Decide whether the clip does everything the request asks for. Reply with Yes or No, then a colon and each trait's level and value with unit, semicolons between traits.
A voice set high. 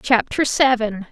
Yes: high, 235 Hz